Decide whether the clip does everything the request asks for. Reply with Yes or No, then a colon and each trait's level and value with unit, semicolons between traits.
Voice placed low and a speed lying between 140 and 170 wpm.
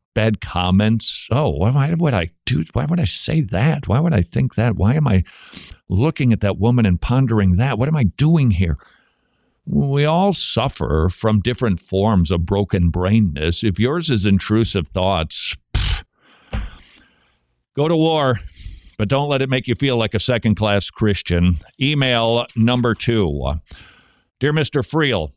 Yes: low, 110 Hz; average, 160 wpm